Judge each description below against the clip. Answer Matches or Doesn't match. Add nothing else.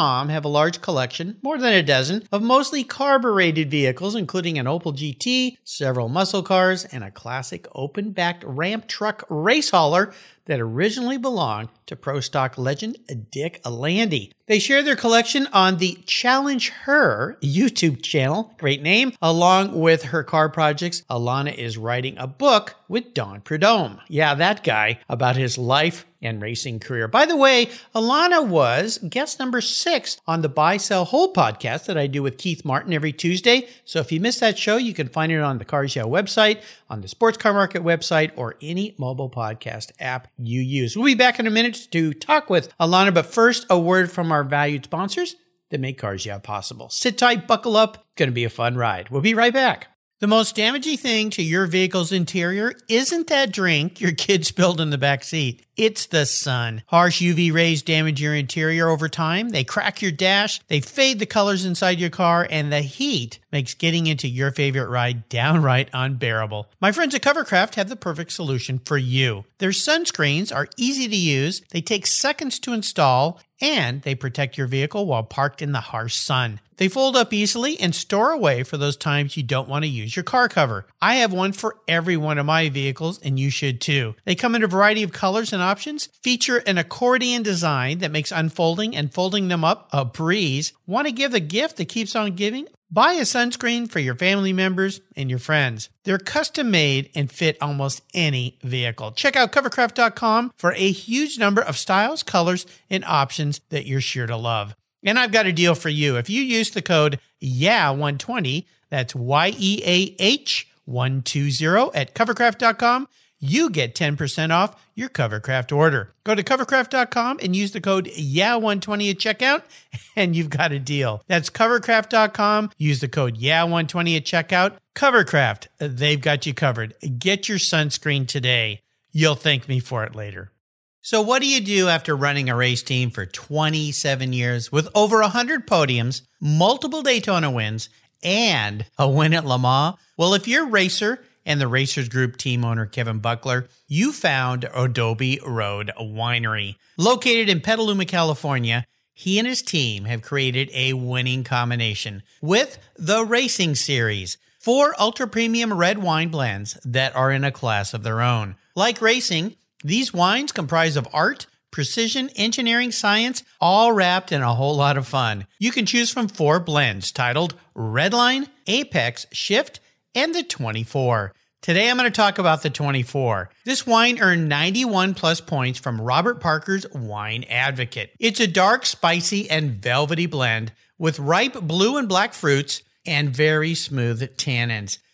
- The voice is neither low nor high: Matches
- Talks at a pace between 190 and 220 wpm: Doesn't match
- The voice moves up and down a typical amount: Doesn't match